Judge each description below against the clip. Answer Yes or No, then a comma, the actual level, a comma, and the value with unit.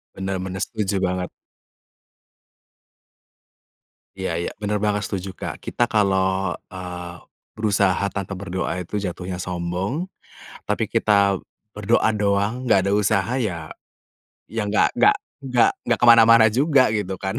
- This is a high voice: No, low, 100 Hz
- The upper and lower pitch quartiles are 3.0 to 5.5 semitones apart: No, narrow, 2.6 semitones